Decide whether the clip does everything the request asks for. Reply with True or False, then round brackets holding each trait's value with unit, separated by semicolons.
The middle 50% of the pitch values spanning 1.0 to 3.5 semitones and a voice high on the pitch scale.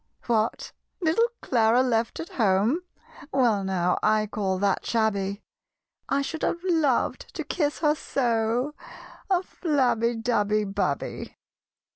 False (5.5 semitones; 230 Hz)